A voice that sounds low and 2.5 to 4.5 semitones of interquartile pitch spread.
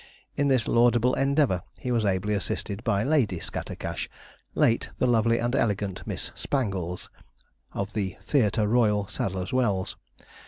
Yes: low, 110 Hz; average, 3.9 semitones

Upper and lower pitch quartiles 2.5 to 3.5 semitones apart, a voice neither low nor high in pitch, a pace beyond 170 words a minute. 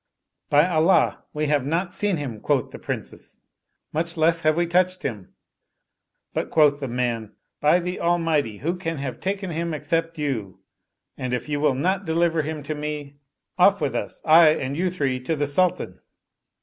Yes: average, 3.2 semitones; medium, 155 Hz; average, 190 wpm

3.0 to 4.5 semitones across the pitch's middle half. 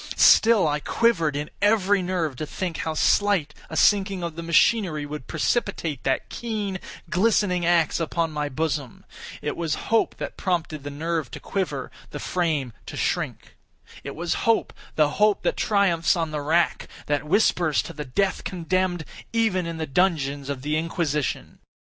Yes: average, 4.1 semitones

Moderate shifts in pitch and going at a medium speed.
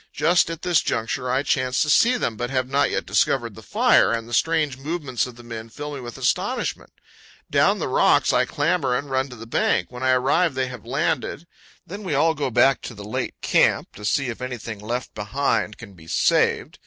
No: average, 3.8 semitones; fast, 215 wpm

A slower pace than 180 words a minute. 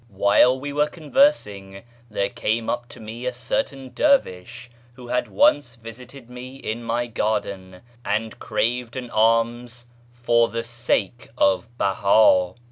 Yes: average, 140 wpm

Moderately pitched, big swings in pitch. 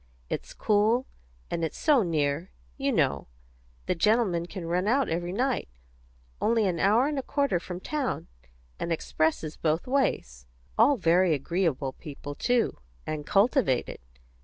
Yes: medium, 180 Hz; wide, 6.7 semitones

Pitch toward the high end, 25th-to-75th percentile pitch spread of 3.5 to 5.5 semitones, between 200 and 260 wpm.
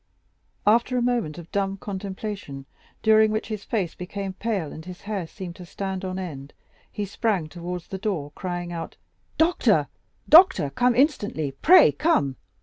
No: high, 195 Hz; average, 4.0 semitones; average, 155 wpm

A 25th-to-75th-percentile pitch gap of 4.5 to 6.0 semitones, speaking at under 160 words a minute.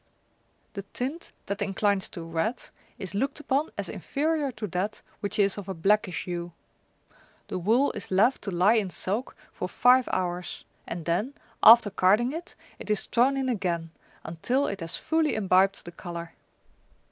No: wide, 5.5 semitones; average, 165 wpm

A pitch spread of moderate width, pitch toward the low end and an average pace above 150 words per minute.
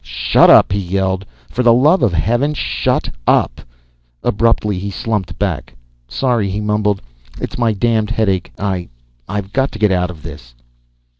Yes: average, 3.5 semitones; low, 100 Hz; average, 160 wpm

